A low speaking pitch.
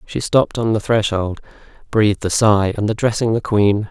Yes: low, 105 Hz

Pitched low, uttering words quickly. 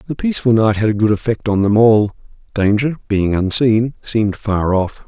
No: low, 110 Hz; average, 190 wpm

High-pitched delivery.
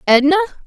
Yes: very high, 325 Hz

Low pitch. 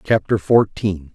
Yes: low, 100 Hz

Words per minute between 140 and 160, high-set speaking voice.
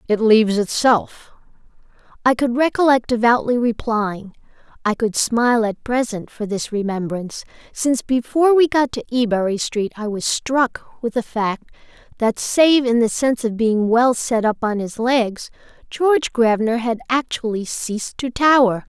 Yes: average, 155 wpm; high, 235 Hz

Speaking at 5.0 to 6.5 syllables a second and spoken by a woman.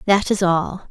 No: 4.2 syllables/s; female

